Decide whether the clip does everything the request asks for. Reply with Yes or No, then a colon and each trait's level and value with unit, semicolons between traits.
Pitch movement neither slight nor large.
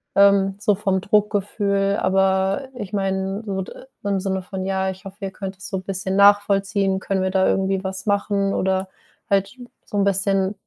No: narrow, 0.9 semitones